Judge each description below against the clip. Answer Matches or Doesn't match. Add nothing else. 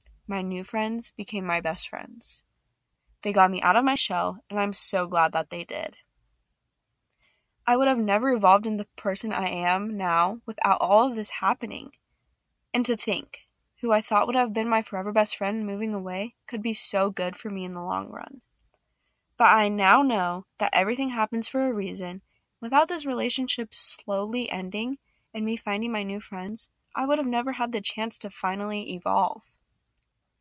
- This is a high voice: Matches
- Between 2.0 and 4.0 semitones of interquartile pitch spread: Matches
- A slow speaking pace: Doesn't match